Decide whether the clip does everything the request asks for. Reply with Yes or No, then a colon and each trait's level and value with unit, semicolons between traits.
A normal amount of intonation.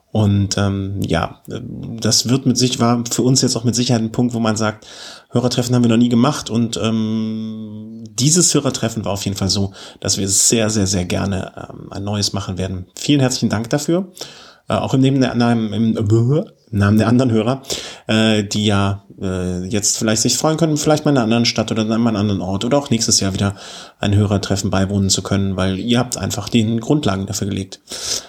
Yes: average, 3.5 semitones